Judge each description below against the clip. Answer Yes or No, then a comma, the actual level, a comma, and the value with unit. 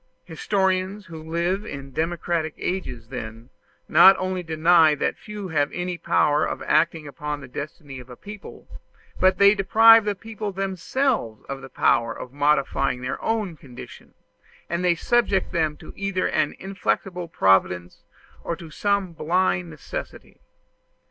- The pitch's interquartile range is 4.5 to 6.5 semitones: Yes, average, 5.0 semitones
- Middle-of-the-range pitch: Yes, medium, 170 Hz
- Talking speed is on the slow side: No, average, 150 wpm